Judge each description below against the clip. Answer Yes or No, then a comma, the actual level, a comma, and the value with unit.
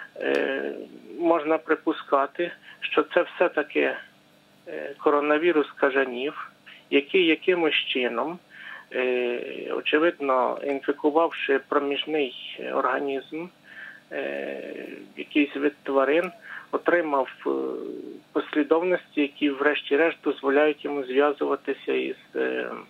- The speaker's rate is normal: No, slow, 65 wpm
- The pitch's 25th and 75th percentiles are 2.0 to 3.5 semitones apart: Yes, narrow, 2.6 semitones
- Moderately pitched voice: Yes, medium, 145 Hz